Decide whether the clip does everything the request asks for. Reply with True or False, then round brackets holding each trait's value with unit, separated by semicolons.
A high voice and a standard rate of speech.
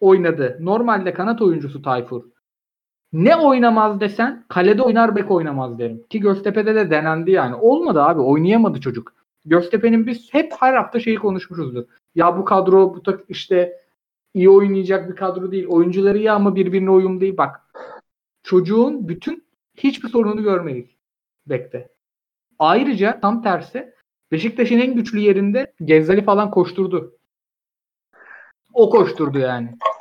True (195 Hz; 130 wpm)